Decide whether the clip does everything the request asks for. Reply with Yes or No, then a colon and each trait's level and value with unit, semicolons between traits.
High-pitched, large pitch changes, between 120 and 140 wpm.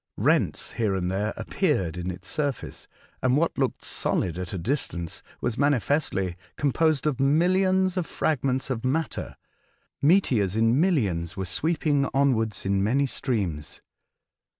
No: low, 130 Hz; wide, 7.3 semitones; slow, 135 wpm